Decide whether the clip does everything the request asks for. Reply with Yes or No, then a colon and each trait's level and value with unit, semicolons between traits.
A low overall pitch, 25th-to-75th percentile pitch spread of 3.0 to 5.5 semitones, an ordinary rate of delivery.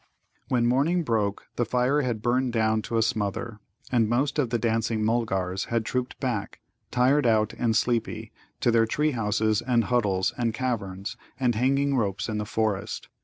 No: low, 115 Hz; narrow, 2.6 semitones; average, 170 wpm